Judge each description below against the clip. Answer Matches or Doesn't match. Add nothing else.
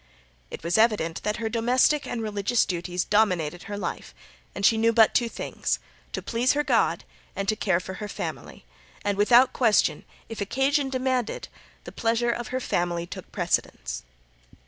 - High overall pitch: Matches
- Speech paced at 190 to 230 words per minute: Doesn't match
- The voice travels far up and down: Doesn't match